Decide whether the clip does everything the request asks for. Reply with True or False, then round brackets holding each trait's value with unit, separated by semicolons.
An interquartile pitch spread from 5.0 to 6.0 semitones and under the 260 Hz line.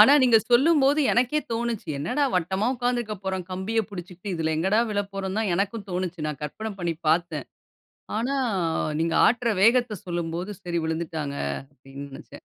True (5.3 semitones; 190 Hz)